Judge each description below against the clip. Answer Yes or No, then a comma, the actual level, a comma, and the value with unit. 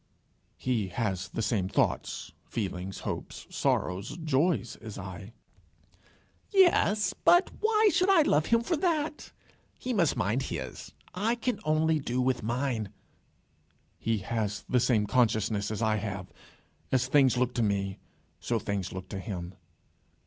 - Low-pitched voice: Yes, low, 120 Hz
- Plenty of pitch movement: Yes, wide, 8.3 semitones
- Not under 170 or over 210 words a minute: No, average, 140 wpm